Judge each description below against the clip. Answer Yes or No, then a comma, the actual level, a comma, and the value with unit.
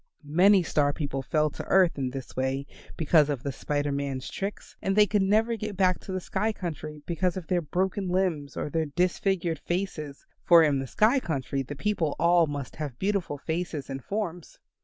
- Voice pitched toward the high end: No, medium, 165 Hz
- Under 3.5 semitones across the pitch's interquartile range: No, average, 5.0 semitones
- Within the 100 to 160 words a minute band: No, average, 195 wpm